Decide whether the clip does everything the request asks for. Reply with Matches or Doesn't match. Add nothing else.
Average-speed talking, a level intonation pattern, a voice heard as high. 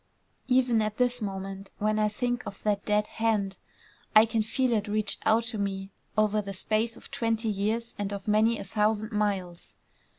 Matches